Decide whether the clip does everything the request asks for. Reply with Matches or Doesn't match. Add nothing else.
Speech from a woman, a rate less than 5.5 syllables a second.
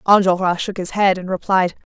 Matches